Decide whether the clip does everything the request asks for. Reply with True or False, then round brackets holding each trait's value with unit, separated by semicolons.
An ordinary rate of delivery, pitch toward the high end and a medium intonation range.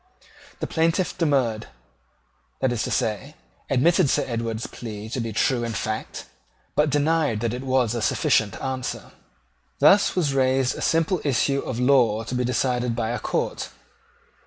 False (160 wpm; 125 Hz; 3.6 semitones)